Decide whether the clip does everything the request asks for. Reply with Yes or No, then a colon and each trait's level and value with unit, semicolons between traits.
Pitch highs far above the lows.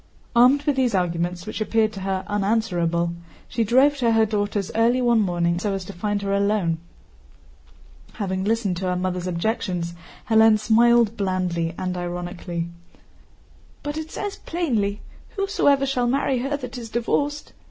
No: average, 4.8 semitones